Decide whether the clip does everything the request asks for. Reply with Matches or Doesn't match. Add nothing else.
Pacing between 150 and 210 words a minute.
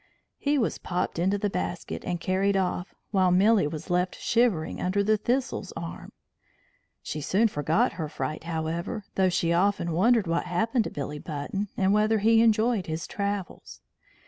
Matches